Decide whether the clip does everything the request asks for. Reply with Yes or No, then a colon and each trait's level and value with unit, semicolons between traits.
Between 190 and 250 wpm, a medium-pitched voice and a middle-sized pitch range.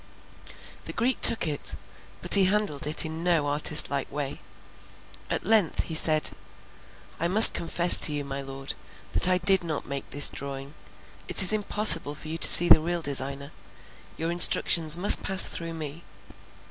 No: average, 170 wpm; medium, 160 Hz; average, 3.6 semitones